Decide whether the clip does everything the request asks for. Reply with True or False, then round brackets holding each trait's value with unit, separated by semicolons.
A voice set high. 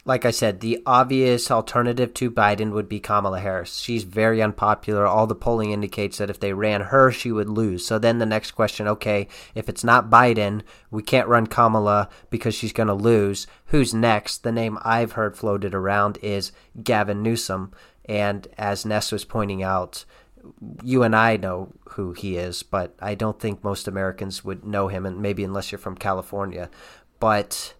False (105 Hz)